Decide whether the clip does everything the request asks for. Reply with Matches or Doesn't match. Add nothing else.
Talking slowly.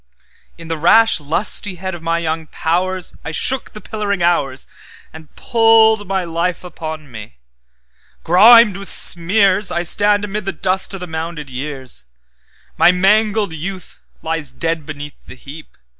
Matches